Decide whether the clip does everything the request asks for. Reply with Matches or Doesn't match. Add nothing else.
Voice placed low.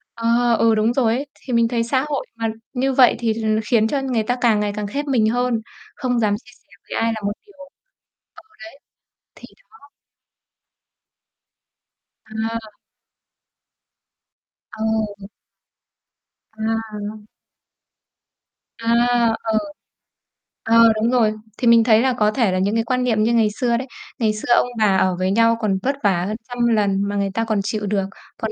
Doesn't match